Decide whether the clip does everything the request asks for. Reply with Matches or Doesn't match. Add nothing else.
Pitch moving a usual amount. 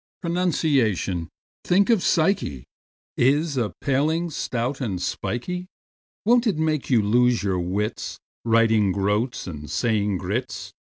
Doesn't match